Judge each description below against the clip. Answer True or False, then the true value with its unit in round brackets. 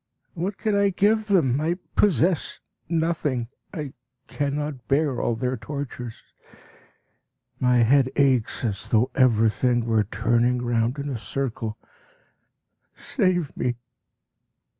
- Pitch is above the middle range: False (130 Hz)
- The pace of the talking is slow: True (115 wpm)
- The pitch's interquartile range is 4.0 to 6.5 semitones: True (5.1 semitones)